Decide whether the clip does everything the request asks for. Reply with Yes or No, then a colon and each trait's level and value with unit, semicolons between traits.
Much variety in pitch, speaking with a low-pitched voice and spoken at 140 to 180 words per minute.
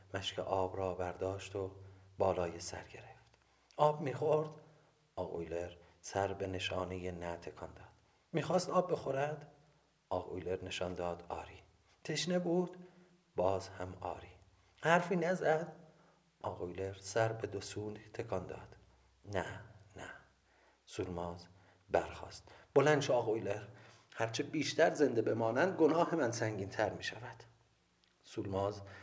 No: wide, 8.3 semitones; low, 100 Hz; average, 115 wpm